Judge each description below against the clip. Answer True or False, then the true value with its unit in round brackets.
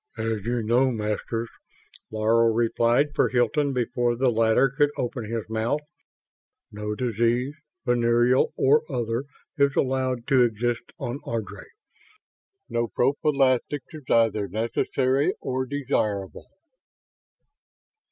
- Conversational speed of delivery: False (110 wpm)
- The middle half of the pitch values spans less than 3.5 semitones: True (2.6 semitones)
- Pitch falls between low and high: False (120 Hz)